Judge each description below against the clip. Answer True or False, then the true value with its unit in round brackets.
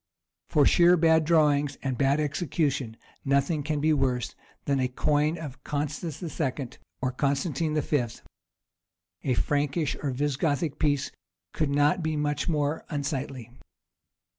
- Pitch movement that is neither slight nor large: False (2.1 semitones)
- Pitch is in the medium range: True (145 Hz)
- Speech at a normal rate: False (130 wpm)